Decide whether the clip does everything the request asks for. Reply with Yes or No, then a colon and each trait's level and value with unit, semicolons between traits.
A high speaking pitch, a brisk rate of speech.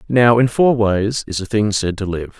No: low, 110 Hz; fast, 250 wpm